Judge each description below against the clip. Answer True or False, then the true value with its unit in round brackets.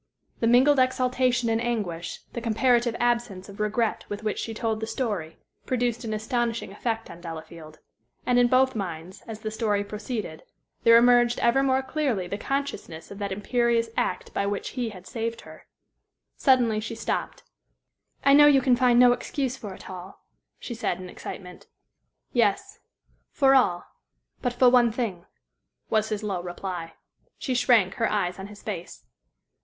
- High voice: True (225 Hz)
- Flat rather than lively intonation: False (3.6 semitones)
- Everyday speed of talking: True (165 wpm)